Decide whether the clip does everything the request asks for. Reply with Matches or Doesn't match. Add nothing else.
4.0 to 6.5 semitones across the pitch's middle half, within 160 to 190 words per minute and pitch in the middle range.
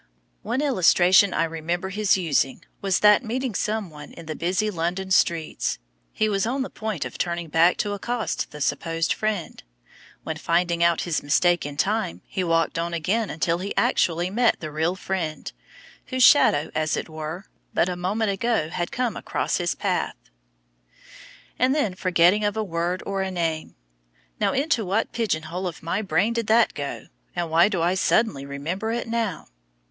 Matches